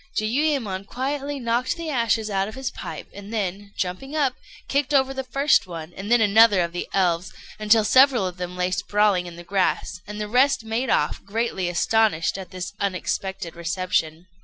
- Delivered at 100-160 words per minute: No, average, 180 wpm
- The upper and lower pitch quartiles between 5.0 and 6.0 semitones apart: Yes, wide, 5.4 semitones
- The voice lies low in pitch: No, high, 210 Hz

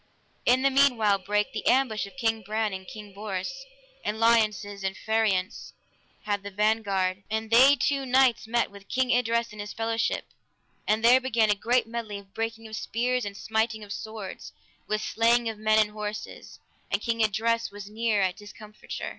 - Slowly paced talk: No, average, 180 wpm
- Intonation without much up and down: Yes, narrow, 2.0 semitones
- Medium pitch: No, high, 220 Hz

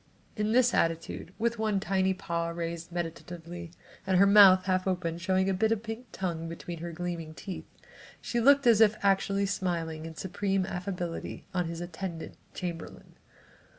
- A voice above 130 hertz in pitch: Yes, medium, 185 Hz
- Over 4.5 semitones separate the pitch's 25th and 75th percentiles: No, average, 2.9 semitones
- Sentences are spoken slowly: No, average, 160 wpm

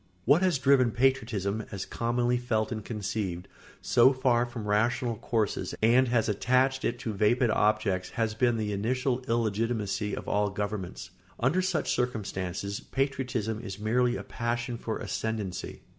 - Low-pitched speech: Yes, low, 115 Hz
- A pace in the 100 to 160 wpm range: Yes, average, 150 wpm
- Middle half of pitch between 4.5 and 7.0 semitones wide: No, average, 3.0 semitones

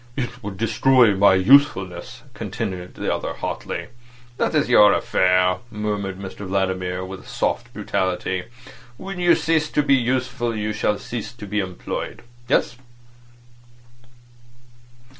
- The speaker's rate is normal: No, slow, 120 wpm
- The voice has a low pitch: Yes, low, 105 Hz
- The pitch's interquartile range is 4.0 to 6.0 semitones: Yes, average, 5.1 semitones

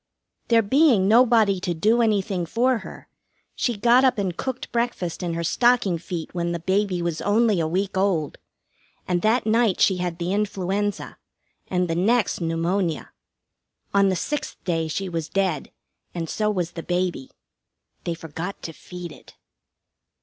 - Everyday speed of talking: Yes, average, 160 wpm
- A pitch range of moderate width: Yes, average, 4.0 semitones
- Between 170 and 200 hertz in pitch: Yes, high, 190 Hz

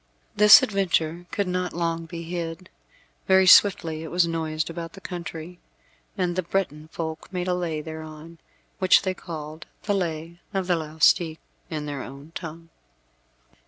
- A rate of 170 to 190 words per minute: No, average, 155 wpm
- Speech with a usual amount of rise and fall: No, narrow, 2.3 semitones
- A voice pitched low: No, medium, 165 Hz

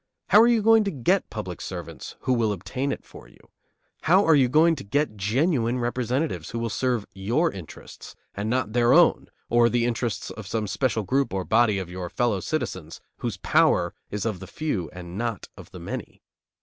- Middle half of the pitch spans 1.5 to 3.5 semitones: No, wide, 5.6 semitones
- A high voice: No, low, 115 Hz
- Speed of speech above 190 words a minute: Yes, average, 200 wpm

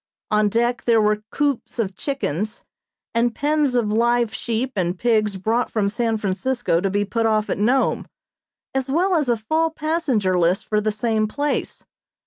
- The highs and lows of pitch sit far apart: No, average, 3.8 semitones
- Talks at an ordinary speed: Yes, average, 170 wpm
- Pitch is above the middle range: Yes, high, 230 Hz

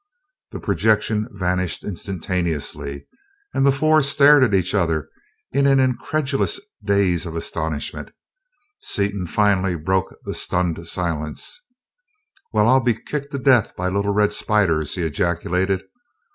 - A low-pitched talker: Yes, low, 100 Hz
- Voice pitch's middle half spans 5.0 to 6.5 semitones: Yes, wide, 5.4 semitones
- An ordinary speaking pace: No, slow, 130 wpm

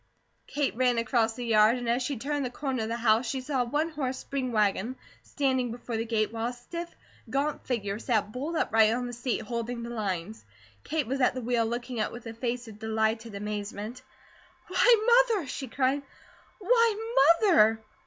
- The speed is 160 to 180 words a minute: No, average, 195 wpm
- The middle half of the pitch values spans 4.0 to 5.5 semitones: No, average, 3.4 semitones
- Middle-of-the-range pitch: No, high, 245 Hz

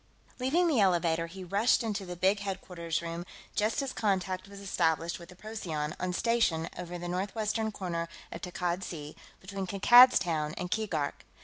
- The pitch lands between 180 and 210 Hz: Yes, medium, 185 Hz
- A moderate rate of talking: Yes, average, 170 wpm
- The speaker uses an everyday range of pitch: Yes, average, 3.6 semitones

